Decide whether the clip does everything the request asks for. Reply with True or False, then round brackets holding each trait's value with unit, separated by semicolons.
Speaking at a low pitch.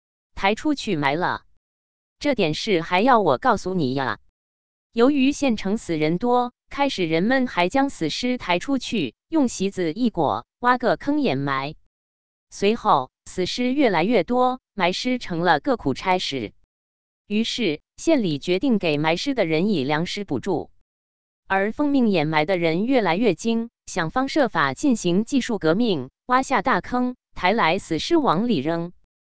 False (190 Hz)